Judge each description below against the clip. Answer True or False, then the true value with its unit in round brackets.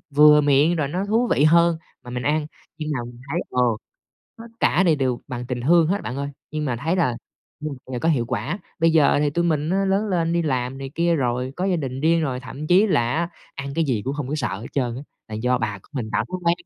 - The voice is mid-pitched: True (150 Hz)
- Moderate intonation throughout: True (4.8 semitones)